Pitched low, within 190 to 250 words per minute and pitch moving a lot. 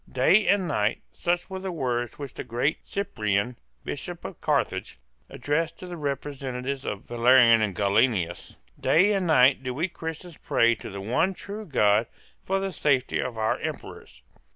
No: low, 130 Hz; average, 165 wpm; wide, 6.8 semitones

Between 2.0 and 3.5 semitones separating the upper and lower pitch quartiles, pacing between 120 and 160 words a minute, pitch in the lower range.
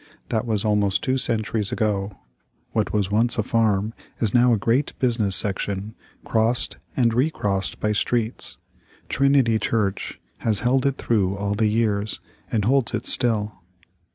Yes: narrow, 2.6 semitones; average, 150 wpm; low, 110 Hz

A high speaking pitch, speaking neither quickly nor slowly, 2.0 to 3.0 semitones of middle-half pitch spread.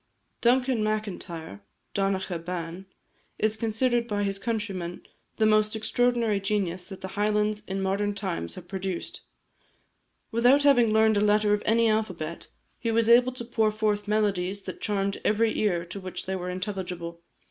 Yes: high, 210 Hz; average, 155 wpm; average, 2.7 semitones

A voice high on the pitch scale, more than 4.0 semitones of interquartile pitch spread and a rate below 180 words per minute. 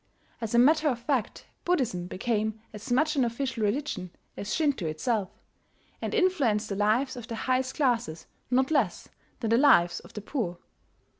Yes: high, 235 Hz; average, 4.5 semitones; average, 165 wpm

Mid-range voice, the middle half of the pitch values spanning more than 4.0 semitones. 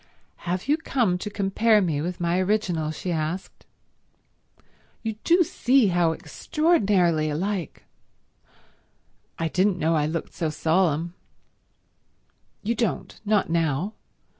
Yes: medium, 180 Hz; average, 4.5 semitones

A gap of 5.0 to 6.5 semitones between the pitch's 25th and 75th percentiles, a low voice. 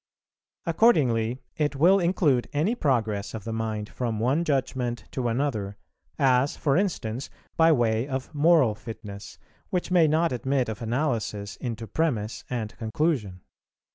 Yes: average, 5.3 semitones; low, 125 Hz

